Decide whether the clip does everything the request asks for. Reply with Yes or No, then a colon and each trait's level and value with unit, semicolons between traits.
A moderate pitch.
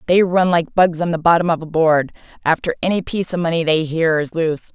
Yes: medium, 165 Hz